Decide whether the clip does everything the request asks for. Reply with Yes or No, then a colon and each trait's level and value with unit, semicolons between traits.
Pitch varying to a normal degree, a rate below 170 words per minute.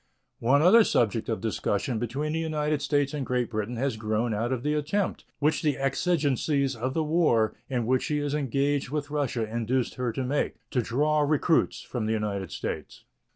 No: average, 4.3 semitones; average, 190 wpm